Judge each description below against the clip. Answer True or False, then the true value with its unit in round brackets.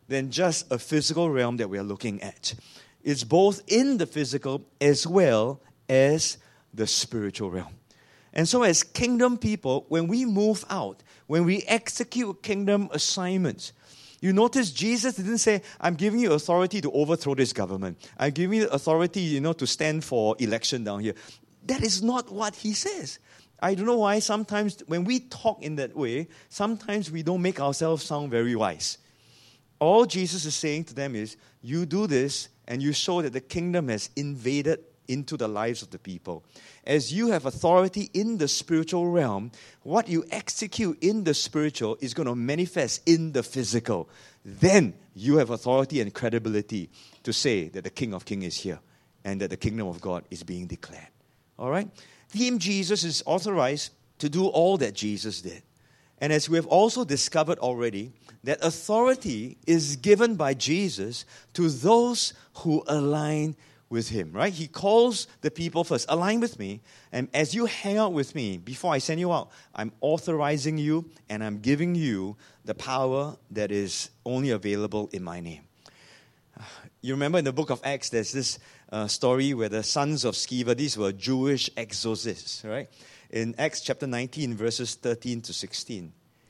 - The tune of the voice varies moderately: False (7.2 semitones)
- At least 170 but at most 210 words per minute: True (175 wpm)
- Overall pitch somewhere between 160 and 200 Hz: False (145 Hz)